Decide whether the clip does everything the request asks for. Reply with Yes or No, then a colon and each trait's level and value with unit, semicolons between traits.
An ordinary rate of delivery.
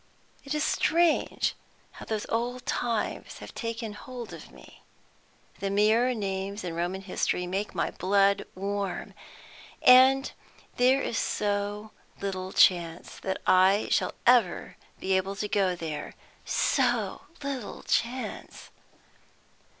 No: slow, 120 wpm